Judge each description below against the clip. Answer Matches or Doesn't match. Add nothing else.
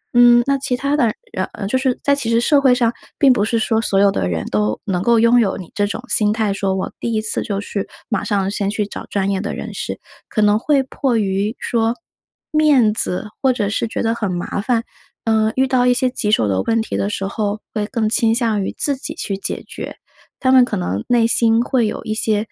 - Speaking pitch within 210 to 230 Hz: Matches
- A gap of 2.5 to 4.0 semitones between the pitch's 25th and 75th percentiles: Matches